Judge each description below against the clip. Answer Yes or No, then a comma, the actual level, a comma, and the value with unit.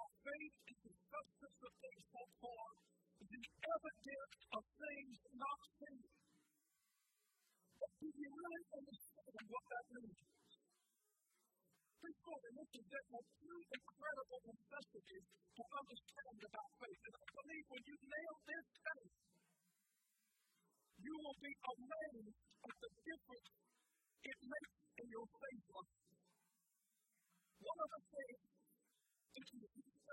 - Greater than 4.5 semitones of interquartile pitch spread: Yes, average, 5.1 semitones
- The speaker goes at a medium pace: No, slow, 125 wpm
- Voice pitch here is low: No, very high, 265 Hz